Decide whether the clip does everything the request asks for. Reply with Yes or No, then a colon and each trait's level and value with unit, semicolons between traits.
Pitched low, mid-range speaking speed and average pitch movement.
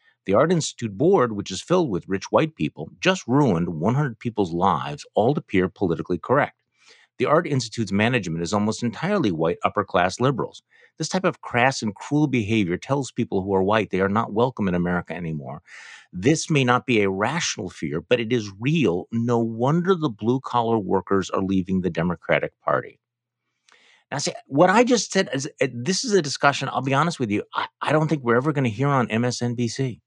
No: low, 120 Hz; average, 195 wpm; wide, 6.1 semitones